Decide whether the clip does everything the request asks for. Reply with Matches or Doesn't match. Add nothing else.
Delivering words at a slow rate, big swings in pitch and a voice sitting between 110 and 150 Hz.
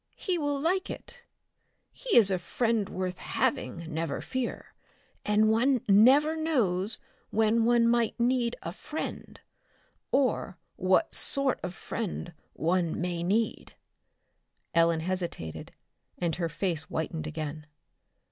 Doesn't match